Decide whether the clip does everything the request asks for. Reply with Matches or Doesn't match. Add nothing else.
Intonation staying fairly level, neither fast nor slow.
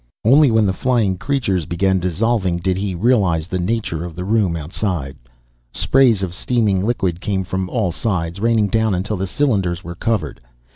Doesn't match